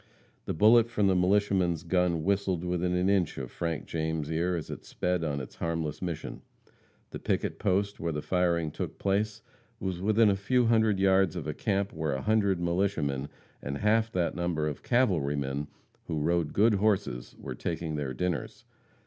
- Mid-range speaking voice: No, very low, 90 Hz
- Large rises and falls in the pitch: No, average, 4.1 semitones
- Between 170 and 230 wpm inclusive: Yes, average, 175 wpm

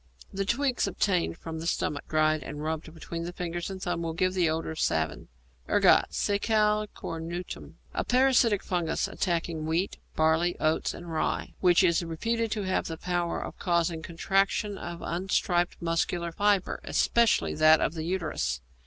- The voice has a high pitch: No, medium, 175 Hz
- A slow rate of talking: No, average, 160 wpm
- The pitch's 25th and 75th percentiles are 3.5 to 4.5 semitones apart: No, average, 3.0 semitones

